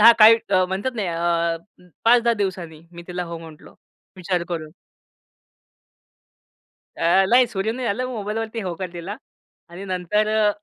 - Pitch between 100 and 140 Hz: No, high, 195 Hz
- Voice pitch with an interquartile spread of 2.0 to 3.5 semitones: No, average, 4.0 semitones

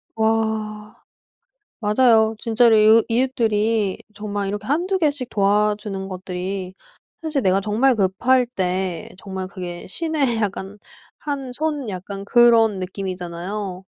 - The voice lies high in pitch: Yes, high, 210 Hz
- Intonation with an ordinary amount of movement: Yes, average, 3.8 semitones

